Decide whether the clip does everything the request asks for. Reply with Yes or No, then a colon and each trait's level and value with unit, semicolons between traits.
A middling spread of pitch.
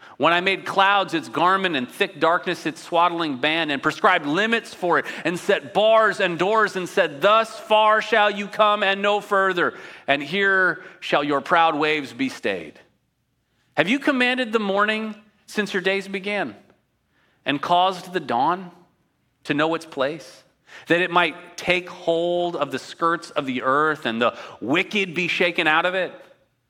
Yes: average, 3.9 semitones